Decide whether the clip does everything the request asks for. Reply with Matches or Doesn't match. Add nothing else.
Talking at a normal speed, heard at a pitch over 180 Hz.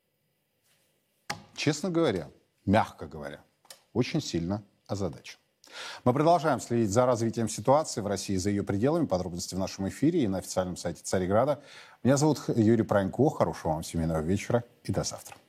Doesn't match